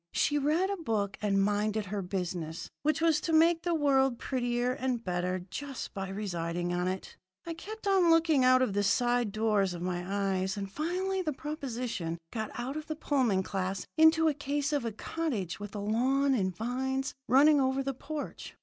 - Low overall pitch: No, high, 245 Hz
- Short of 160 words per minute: No, average, 190 wpm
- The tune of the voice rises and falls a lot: Yes, wide, 7.2 semitones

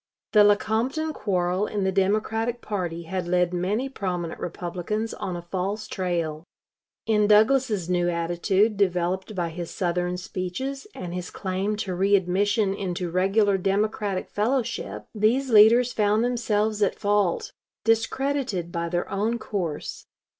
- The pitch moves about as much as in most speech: Yes, average, 3.4 semitones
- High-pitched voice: Yes, high, 195 Hz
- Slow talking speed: Yes, slow, 130 wpm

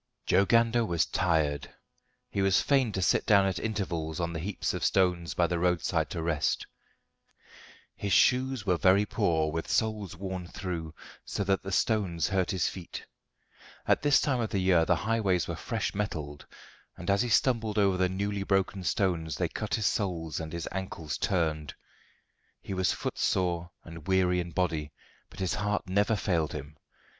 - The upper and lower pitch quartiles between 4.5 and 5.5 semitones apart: No, average, 3.3 semitones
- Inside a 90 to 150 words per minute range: No, average, 175 wpm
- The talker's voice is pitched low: Yes, very low, 95 Hz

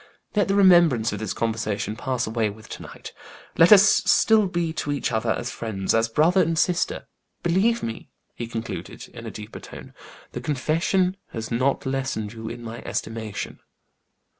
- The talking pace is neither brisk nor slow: Yes, average, 170 wpm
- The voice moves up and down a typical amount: No, wide, 7.5 semitones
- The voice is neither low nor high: No, low, 125 Hz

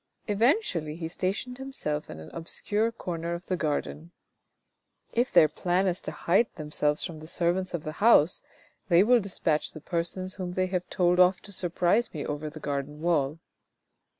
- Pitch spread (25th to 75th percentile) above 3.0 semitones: Yes, average, 3.7 semitones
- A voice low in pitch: No, medium, 175 Hz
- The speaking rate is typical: Yes, average, 180 wpm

